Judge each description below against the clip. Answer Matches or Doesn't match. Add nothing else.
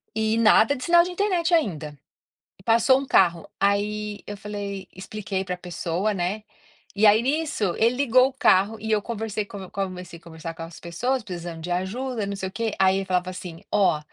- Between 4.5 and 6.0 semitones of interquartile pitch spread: Doesn't match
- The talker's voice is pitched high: Matches